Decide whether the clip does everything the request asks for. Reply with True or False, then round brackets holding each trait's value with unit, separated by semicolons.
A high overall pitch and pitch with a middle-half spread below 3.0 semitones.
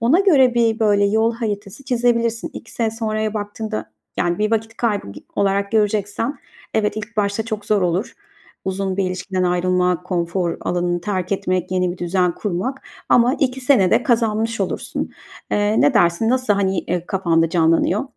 False (205 Hz; 3.7 semitones)